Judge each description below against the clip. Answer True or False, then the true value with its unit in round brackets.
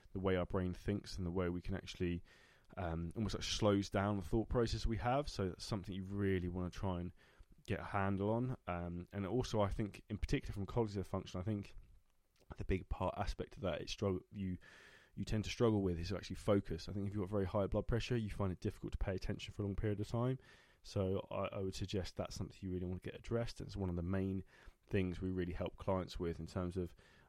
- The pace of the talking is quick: True (245 wpm)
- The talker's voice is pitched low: True (95 Hz)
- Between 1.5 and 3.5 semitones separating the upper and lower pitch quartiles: True (2.5 semitones)